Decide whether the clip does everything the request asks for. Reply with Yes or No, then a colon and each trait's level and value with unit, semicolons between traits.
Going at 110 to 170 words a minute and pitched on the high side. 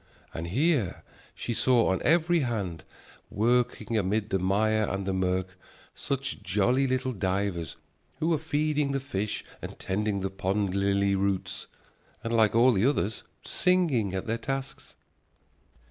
No: average, 145 wpm; low, 110 Hz